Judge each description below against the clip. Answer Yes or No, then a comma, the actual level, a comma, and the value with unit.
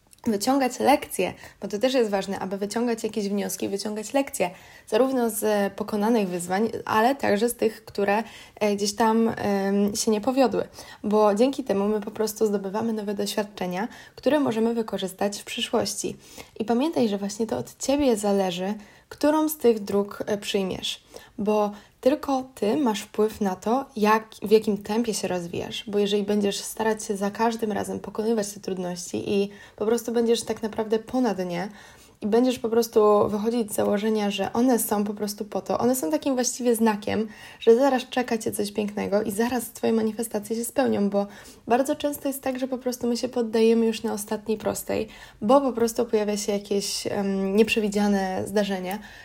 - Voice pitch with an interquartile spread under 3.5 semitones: Yes, narrow, 2.4 semitones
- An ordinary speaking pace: No, fast, 170 wpm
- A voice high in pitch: Yes, high, 220 Hz